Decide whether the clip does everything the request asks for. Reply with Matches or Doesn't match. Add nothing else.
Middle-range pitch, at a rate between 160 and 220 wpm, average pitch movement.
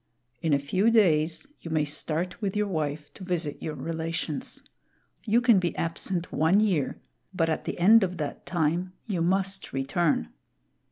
Matches